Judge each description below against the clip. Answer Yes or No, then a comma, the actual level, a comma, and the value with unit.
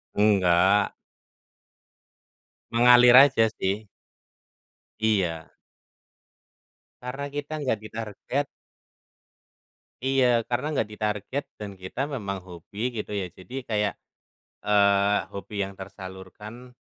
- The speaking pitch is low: Yes, low, 105 Hz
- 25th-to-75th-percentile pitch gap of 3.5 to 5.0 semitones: Yes, average, 3.9 semitones